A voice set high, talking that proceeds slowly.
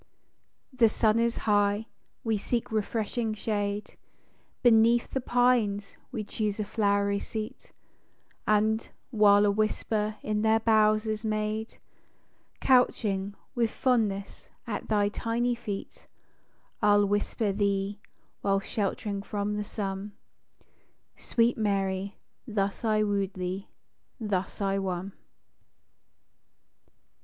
Yes: high, 210 Hz; slow, 110 wpm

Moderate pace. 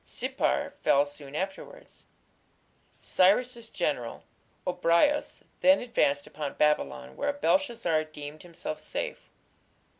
No: slow, 95 wpm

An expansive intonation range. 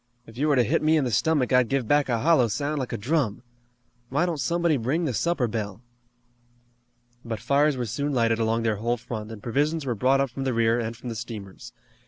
No: average, 4.2 semitones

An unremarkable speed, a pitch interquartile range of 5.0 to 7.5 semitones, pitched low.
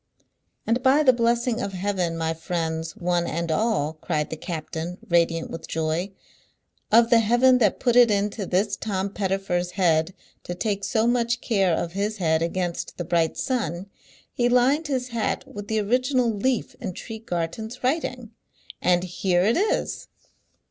No: average, 160 wpm; wide, 5.4 semitones; high, 200 Hz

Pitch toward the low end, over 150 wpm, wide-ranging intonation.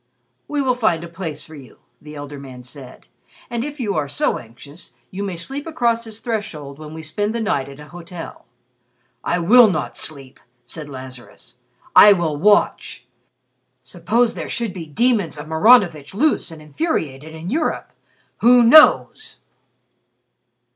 No: medium, 170 Hz; average, 160 wpm; wide, 7.6 semitones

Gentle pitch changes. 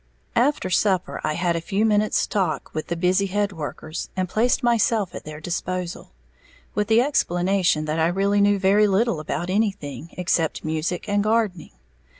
No: average, 3.5 semitones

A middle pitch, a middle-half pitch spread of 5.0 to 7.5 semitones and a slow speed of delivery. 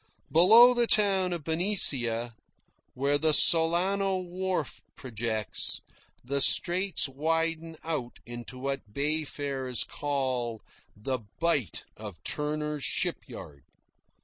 Yes: medium, 150 Hz; average, 5.3 semitones; slow, 100 wpm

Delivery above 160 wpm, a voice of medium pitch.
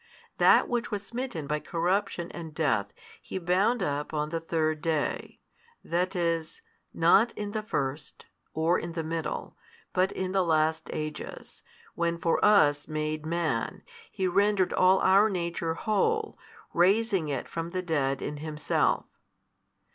No: average, 145 wpm; medium, 170 Hz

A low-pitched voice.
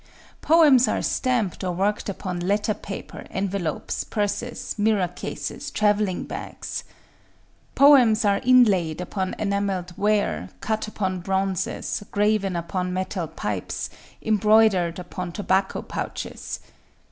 No: high, 200 Hz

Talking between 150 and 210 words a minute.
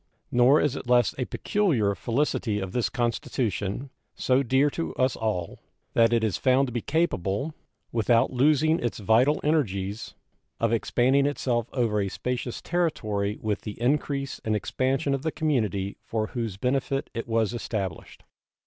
Yes: average, 155 wpm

